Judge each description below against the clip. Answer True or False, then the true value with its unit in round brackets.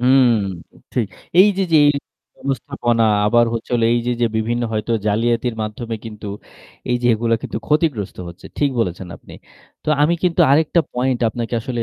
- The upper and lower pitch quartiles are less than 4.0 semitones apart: True (3.0 semitones)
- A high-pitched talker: False (120 Hz)